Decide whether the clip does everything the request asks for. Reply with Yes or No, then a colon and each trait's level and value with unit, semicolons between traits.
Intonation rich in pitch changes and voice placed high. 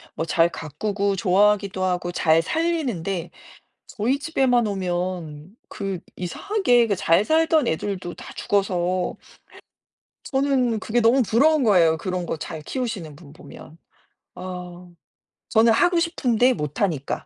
Yes: wide, 5.7 semitones; high, 195 Hz